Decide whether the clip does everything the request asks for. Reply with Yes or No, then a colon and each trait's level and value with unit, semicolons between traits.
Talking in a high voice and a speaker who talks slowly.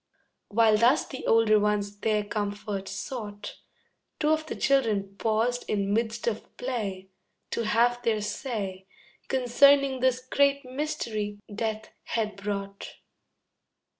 Yes: high, 220 Hz; slow, 120 wpm